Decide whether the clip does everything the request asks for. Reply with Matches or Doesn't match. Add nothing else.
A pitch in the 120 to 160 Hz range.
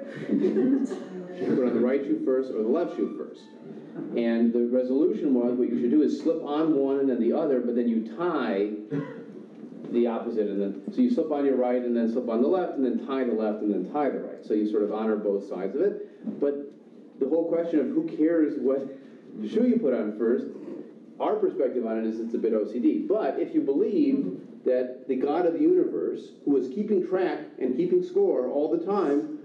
Matches